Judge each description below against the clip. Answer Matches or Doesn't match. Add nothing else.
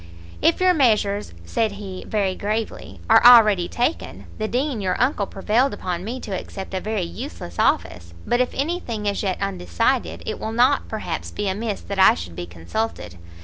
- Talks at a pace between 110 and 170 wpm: Doesn't match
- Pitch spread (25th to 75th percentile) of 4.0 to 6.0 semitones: Matches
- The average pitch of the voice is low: Doesn't match